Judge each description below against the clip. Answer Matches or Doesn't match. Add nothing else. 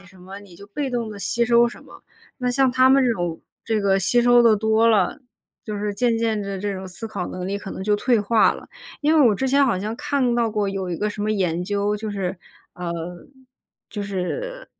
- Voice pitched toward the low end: Doesn't match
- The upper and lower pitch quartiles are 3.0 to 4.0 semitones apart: Matches